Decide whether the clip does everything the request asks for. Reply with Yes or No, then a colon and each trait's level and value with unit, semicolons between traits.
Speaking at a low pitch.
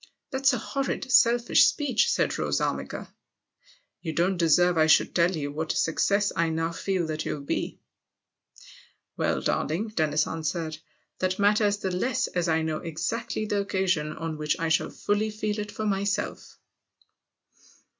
No: medium, 180 Hz